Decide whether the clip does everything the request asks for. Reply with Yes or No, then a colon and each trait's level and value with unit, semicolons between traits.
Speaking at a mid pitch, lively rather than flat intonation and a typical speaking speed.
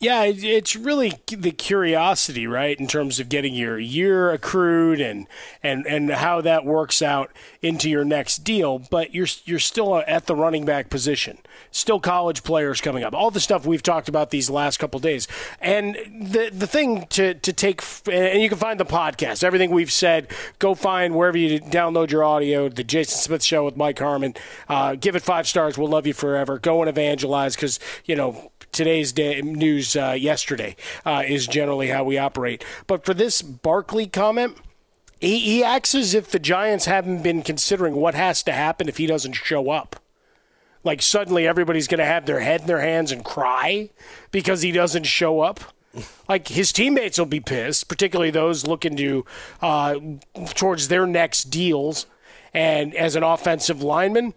No: medium, 165 Hz; average, 4.4 semitones; average, 185 wpm